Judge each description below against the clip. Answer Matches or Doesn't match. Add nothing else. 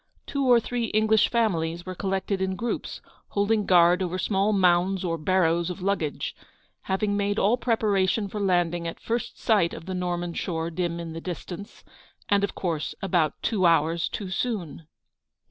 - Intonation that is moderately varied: Matches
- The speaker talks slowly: Doesn't match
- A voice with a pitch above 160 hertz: Matches